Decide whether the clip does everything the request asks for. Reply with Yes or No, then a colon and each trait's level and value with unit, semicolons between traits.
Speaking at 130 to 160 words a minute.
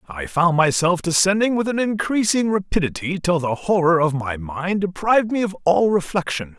No: average, 175 wpm